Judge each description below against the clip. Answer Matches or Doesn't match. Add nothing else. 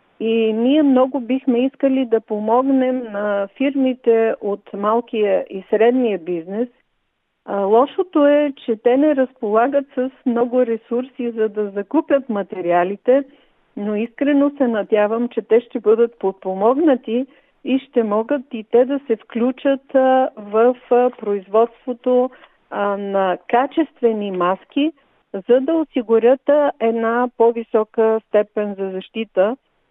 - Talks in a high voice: Matches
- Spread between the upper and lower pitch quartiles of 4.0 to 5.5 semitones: Doesn't match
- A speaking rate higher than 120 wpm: Doesn't match